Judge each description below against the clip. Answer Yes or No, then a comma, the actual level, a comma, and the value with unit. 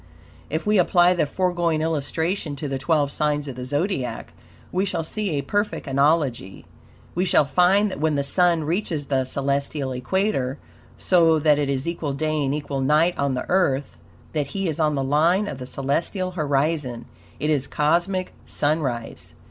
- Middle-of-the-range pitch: Yes, medium, 150 Hz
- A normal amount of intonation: Yes, average, 3.9 semitones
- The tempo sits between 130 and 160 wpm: No, average, 170 wpm